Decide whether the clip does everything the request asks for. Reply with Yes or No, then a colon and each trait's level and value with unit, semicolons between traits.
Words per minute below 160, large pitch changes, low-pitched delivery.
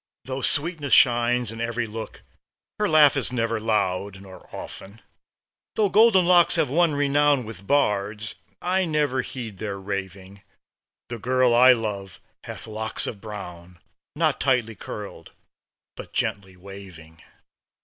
Yes: slow, 135 wpm; wide, 5.9 semitones; low, 115 Hz